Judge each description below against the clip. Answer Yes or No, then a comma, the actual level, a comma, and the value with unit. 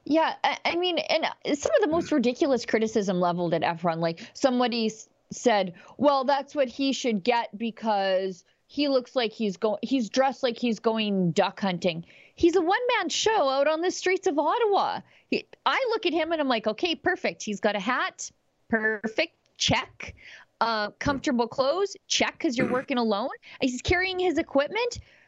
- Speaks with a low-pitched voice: No, very high, 255 Hz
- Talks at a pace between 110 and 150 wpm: No, average, 175 wpm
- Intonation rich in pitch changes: Yes, wide, 7.0 semitones